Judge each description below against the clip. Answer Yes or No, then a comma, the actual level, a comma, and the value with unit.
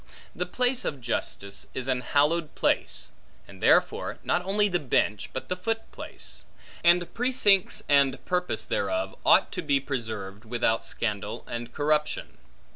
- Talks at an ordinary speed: Yes, average, 145 wpm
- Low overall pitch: No, medium, 145 Hz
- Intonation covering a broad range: Yes, wide, 7.4 semitones